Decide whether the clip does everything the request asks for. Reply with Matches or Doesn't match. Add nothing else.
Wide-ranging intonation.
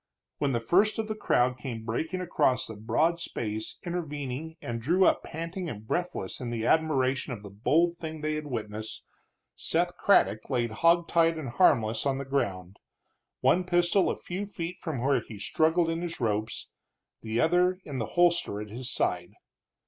Matches